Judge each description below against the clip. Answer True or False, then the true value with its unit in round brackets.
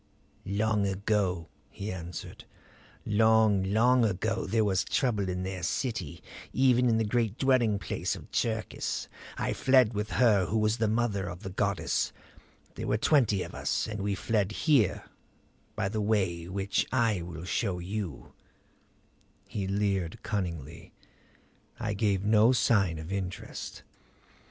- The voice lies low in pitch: True (105 Hz)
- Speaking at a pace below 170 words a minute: True (145 wpm)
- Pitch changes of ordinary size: True (3.0 semitones)